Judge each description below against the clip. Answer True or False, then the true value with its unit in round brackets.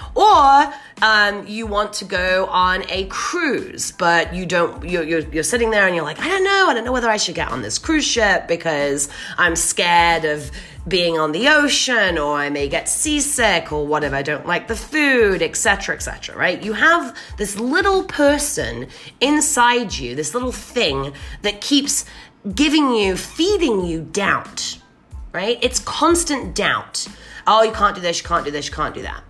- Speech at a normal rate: True (190 wpm)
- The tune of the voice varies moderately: False (8.9 semitones)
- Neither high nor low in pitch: False (210 Hz)